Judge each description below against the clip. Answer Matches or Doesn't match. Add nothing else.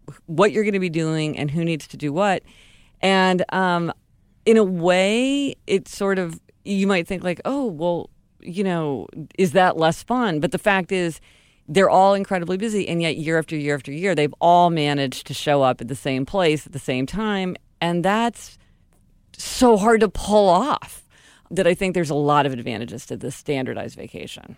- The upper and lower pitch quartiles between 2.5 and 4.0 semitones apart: Doesn't match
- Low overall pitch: Doesn't match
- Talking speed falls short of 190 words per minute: Doesn't match